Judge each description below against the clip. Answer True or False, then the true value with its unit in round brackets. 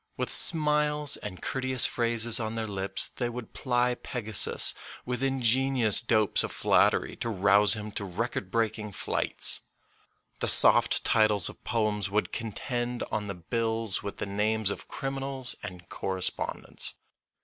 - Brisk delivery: False (145 wpm)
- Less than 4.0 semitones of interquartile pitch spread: True (3.2 semitones)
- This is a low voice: True (110 Hz)